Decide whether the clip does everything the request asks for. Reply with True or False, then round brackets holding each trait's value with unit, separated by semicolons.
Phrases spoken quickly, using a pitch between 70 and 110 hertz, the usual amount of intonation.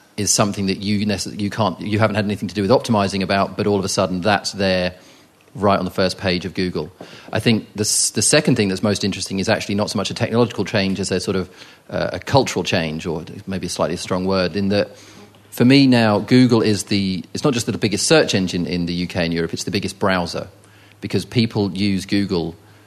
False (235 wpm; 100 Hz; 1.9 semitones)